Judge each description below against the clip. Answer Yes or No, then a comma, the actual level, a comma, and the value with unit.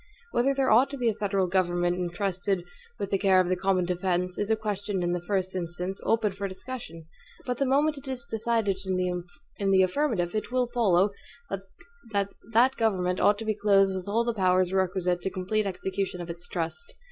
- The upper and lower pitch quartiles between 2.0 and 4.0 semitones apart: Yes, average, 3.4 semitones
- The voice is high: Yes, high, 195 Hz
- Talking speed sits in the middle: Yes, average, 195 wpm